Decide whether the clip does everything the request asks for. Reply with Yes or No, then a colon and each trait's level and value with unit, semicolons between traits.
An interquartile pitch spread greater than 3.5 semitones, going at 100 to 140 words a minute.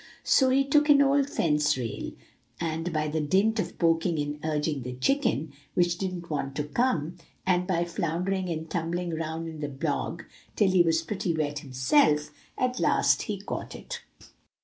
No: average, 4.0 semitones; average, 170 wpm